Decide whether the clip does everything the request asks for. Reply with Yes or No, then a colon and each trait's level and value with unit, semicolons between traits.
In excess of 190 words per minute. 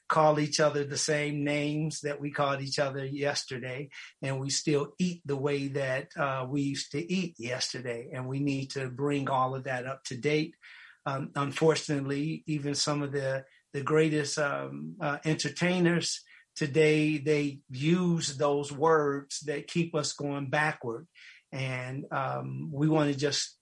No: average, 160 wpm